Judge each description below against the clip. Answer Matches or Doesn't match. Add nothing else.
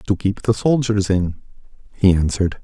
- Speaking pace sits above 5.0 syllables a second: Matches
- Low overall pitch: Matches